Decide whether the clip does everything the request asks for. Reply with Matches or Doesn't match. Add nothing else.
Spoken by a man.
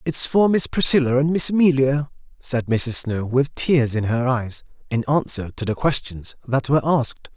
Matches